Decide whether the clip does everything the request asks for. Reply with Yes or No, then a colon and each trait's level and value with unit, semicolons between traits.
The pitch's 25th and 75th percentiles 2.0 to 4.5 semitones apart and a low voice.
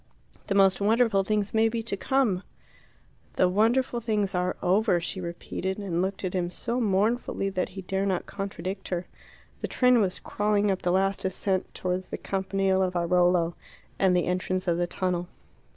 No: narrow, 2.4 semitones; high, 190 Hz